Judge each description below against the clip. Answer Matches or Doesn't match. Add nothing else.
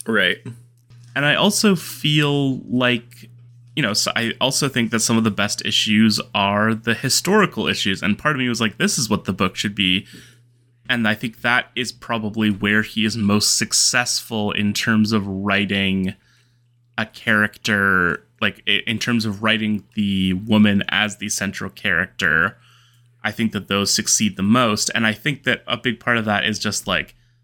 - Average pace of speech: Matches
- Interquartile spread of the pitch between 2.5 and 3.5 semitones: Matches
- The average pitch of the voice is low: Matches